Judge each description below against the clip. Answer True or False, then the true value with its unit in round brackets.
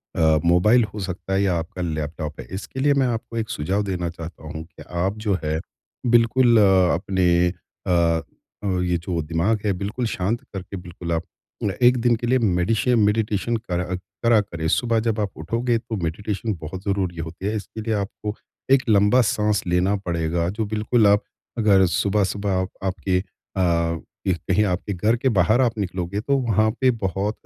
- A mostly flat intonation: False (4.1 semitones)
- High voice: False (100 Hz)